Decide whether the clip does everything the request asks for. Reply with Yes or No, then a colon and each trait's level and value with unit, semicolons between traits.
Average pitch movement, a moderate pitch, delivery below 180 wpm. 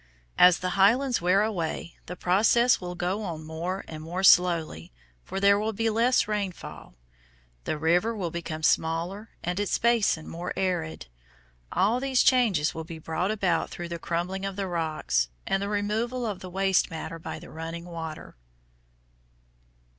Yes: average, 3.8 semitones; medium, 180 Hz; average, 160 wpm